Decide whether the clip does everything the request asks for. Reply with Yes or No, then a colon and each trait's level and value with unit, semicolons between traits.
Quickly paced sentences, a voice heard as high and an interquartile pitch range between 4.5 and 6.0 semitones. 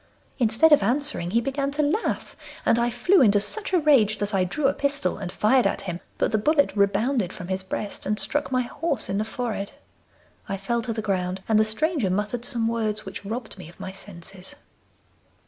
Yes: fast, 210 wpm; high, 220 Hz; wide, 5.4 semitones